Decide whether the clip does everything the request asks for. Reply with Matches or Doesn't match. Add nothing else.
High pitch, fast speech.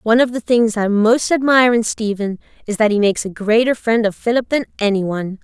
Matches